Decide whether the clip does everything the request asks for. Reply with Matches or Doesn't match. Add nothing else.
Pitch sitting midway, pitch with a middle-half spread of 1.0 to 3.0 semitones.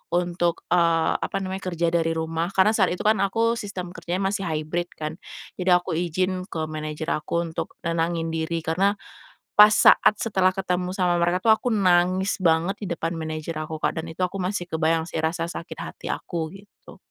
Matches